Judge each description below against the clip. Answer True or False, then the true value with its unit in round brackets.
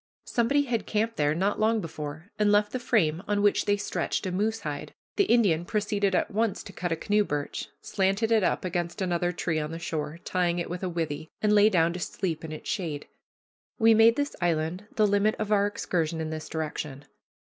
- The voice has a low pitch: False (185 Hz)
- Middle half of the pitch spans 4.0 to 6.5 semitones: True (4.6 semitones)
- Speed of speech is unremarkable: False (210 wpm)